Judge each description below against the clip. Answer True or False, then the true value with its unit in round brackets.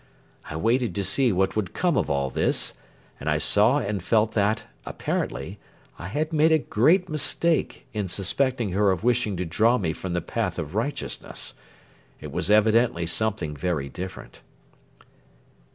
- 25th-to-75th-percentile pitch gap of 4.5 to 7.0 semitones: True (5.6 semitones)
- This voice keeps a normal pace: True (160 wpm)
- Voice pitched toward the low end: True (105 Hz)